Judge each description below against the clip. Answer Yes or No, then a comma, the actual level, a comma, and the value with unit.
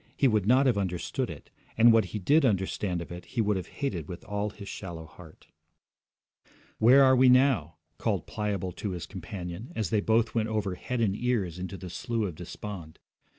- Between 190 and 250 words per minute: Yes, average, 195 wpm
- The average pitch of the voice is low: Yes, low, 105 Hz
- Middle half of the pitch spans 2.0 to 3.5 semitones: No, average, 4.5 semitones